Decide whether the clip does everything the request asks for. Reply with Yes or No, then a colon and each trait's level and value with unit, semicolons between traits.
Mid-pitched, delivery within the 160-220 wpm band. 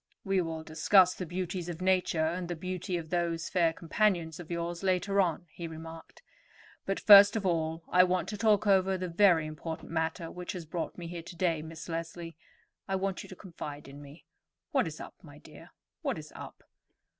Yes: medium, 175 Hz; average, 195 wpm